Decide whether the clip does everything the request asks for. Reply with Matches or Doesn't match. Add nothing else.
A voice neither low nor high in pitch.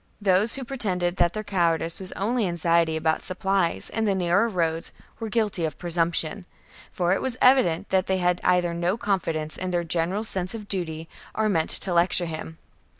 Matches